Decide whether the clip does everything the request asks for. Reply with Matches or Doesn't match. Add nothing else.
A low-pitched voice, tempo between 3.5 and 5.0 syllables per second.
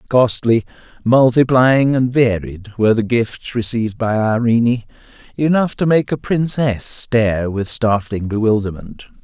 Matches